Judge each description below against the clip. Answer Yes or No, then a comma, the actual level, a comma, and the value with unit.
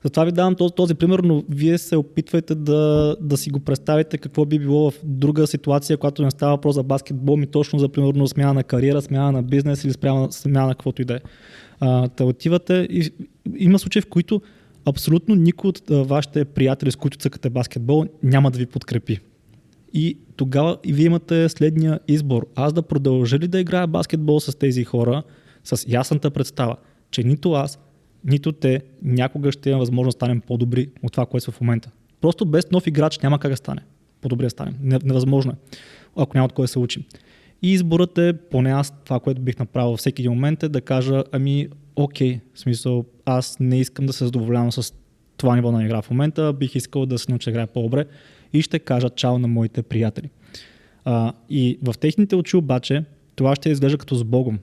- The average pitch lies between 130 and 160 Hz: Yes, medium, 140 Hz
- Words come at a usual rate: No, fast, 200 wpm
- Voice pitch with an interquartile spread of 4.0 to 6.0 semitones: No, average, 3.2 semitones